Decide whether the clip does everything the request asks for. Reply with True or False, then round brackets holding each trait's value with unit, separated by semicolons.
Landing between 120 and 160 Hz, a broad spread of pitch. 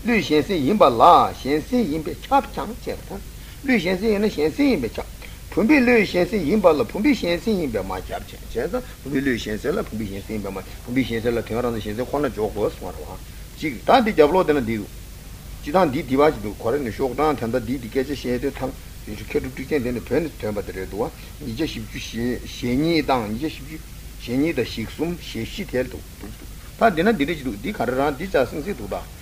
True (125 Hz; 6.3 semitones)